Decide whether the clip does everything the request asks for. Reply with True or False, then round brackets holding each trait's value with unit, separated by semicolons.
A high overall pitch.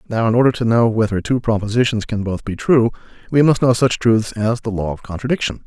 False (115 Hz)